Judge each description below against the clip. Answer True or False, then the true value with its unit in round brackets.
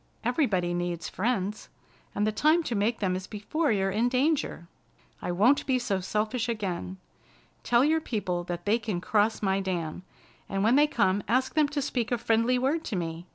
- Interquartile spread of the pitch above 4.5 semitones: True (5.1 semitones)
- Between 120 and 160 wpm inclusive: False (190 wpm)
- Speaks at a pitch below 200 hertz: False (215 Hz)